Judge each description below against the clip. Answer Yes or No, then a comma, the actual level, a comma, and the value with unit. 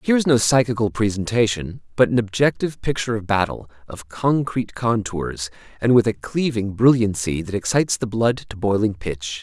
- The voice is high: No, low, 110 Hz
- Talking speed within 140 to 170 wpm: Yes, average, 165 wpm